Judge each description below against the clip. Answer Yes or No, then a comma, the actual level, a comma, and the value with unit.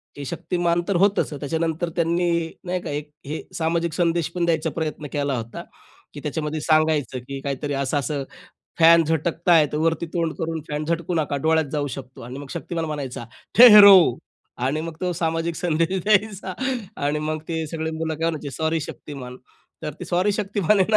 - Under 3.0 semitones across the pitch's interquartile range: Yes, narrow, 2.4 semitones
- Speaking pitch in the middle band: Yes, medium, 160 Hz